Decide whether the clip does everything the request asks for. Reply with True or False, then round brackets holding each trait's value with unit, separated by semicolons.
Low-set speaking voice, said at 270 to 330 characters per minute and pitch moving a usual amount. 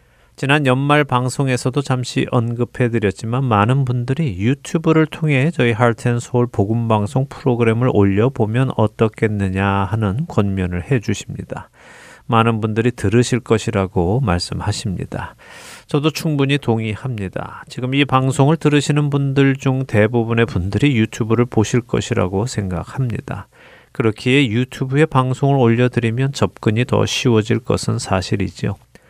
True (120 Hz; 320 characters per minute; 3.7 semitones)